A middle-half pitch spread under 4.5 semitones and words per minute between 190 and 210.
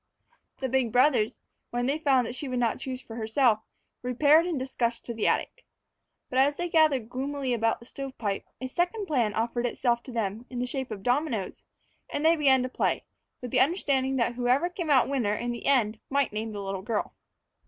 Yes: average, 3.2 semitones; fast, 205 wpm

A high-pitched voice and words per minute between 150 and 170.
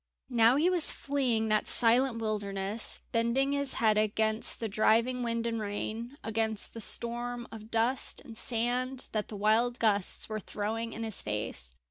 Yes: high, 225 Hz; average, 160 wpm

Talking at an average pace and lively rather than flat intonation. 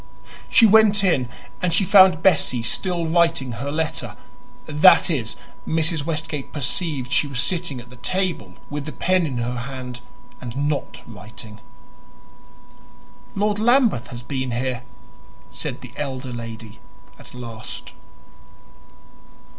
No: slow, 130 wpm; wide, 5.7 semitones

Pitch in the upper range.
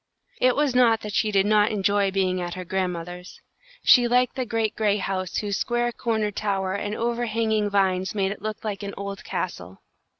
Yes: high, 205 Hz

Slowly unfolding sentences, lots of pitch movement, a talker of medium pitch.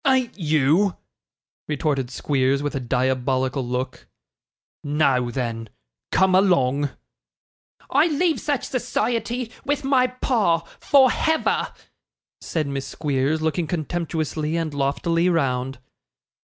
Yes: slow, 105 wpm; wide, 7.2 semitones; medium, 155 Hz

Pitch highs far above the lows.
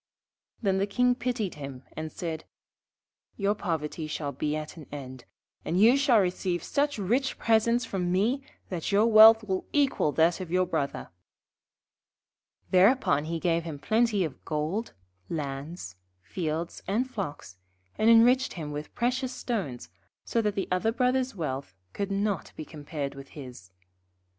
Yes: wide, 6.8 semitones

